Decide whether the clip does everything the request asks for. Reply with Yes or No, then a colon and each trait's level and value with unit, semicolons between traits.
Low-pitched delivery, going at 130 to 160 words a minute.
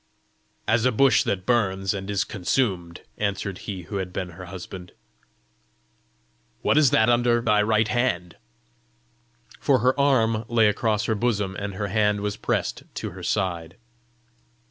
Yes: low, 105 Hz; average, 155 wpm